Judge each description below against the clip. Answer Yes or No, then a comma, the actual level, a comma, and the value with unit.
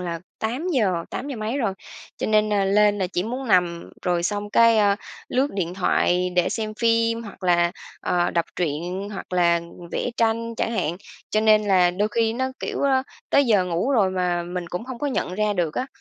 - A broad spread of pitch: No, average, 4.4 semitones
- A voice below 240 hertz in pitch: Yes, high, 205 Hz